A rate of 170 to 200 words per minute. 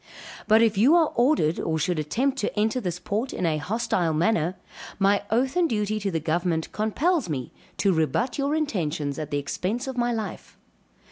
Yes: average, 190 wpm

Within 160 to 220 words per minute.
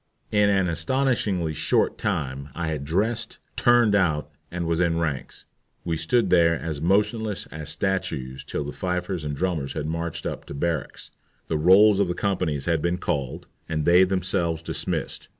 Yes: average, 170 wpm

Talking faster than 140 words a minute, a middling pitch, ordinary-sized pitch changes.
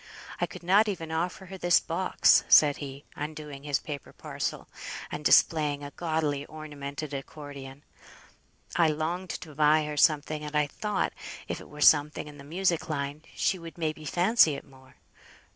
No: average, 170 wpm; medium, 150 Hz; narrow, 2.3 semitones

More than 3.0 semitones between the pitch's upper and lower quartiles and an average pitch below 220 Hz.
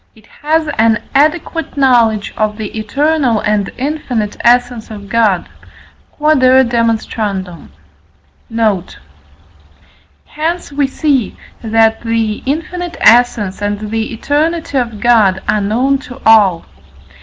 No: average, 4.7 semitones; high, 230 Hz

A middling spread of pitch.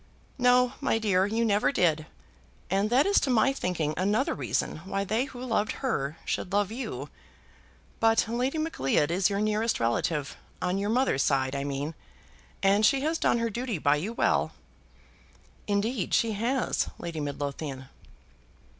No: wide, 6.8 semitones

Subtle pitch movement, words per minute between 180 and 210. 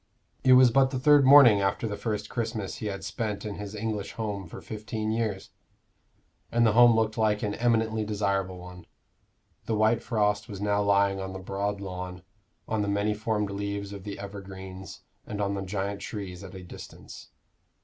Yes: narrow, 2.1 semitones; average, 185 wpm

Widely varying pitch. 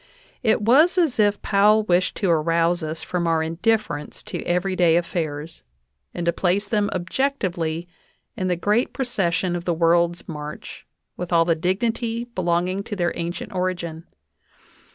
No: average, 3.5 semitones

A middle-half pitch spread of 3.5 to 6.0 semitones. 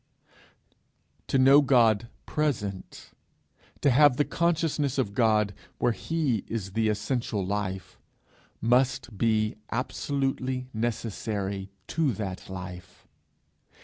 Yes: average, 4.7 semitones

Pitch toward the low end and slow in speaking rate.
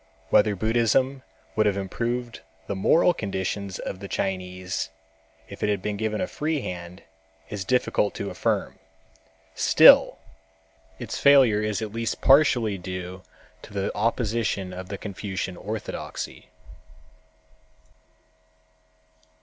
Yes: low, 105 Hz; slow, 115 wpm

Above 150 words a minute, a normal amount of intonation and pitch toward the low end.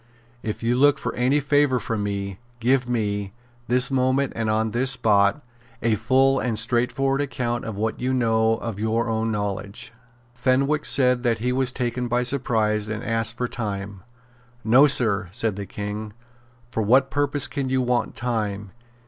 Yes: average, 165 wpm; average, 3.2 semitones; low, 120 Hz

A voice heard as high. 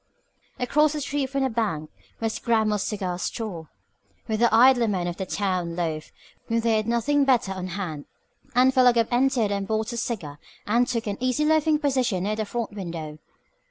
Yes: high, 220 Hz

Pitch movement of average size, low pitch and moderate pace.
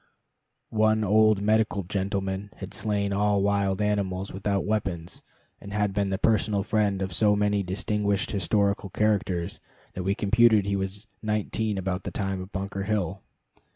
No: narrow, 1.6 semitones; low, 100 Hz; average, 155 wpm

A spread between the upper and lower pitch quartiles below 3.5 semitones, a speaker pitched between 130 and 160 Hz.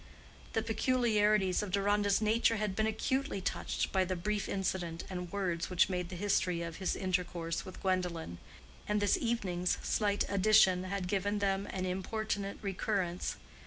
No: narrow, 2.5 semitones; high, 195 Hz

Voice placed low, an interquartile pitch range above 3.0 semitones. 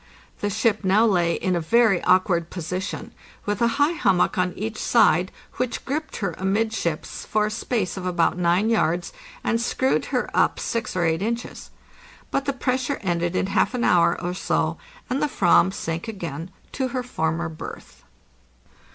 No: high, 195 Hz; average, 5.1 semitones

